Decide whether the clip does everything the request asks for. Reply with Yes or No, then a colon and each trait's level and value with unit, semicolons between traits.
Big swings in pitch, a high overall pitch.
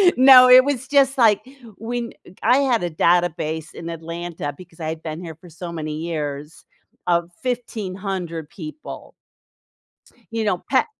No: wide, 6.9 semitones; medium, 175 Hz